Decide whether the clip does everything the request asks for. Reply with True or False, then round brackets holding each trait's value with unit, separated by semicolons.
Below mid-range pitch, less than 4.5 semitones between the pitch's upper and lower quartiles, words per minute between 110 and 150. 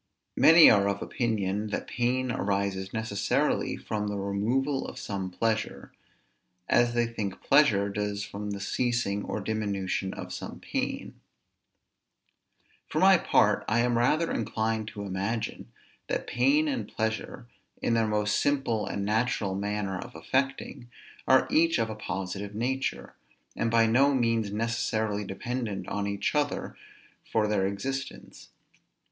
True (110 Hz; 3.2 semitones; 140 wpm)